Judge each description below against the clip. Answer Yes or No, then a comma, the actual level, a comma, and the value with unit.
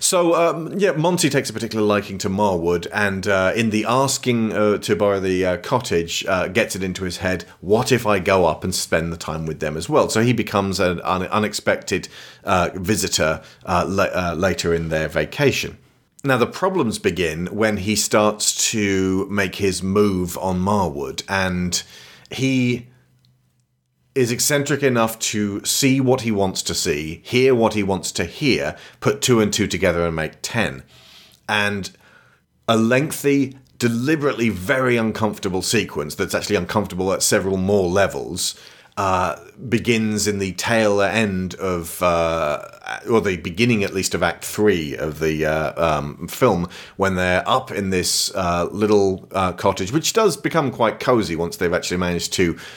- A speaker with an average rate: Yes, average, 165 wpm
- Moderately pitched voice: No, low, 105 Hz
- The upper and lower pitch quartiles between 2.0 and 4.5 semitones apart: No, average, 4.9 semitones